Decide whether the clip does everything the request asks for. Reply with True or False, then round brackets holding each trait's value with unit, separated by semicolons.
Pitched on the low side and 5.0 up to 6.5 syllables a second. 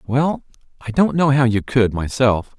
False (125 Hz; 4.3 syllables/s)